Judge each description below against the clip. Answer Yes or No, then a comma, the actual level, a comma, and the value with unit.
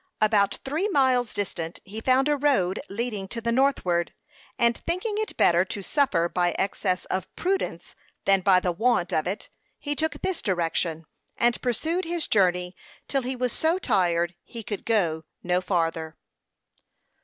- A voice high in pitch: Yes, high, 205 Hz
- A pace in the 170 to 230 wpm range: No, average, 160 wpm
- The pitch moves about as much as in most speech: No, wide, 6.9 semitones